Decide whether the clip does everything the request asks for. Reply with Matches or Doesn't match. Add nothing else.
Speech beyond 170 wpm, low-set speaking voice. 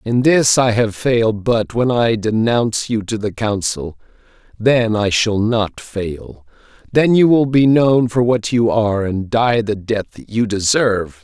Matches